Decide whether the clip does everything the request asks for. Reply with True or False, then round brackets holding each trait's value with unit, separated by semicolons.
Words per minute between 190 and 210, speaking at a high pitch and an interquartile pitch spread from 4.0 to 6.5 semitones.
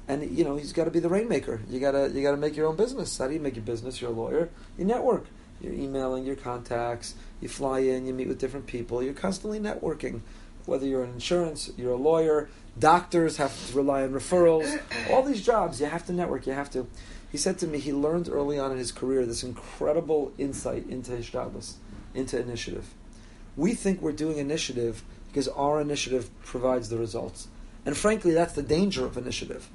False (205 wpm; 140 Hz; 4.4 semitones)